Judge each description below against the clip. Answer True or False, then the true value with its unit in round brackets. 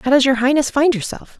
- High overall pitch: True (270 Hz)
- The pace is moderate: False (260 wpm)